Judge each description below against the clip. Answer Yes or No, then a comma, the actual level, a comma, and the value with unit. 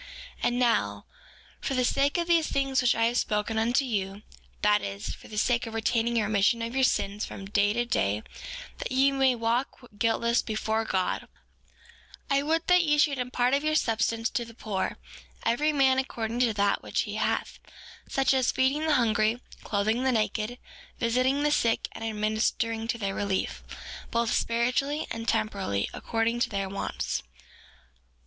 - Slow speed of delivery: No, average, 170 wpm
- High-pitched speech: Yes, high, 230 Hz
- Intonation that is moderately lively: Yes, average, 3.4 semitones